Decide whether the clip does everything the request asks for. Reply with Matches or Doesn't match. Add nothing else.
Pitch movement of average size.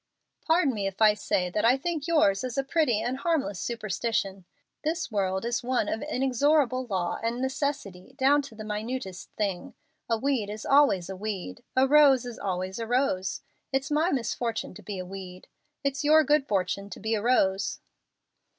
Doesn't match